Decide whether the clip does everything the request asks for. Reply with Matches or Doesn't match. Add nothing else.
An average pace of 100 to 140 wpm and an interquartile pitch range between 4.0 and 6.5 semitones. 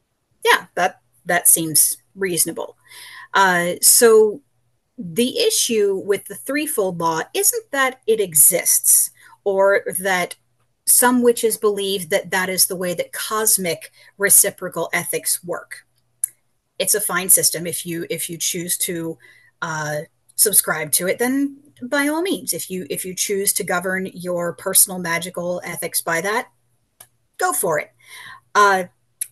Matches